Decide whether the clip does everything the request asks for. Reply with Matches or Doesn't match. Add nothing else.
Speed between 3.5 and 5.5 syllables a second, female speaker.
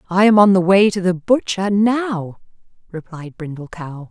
Matches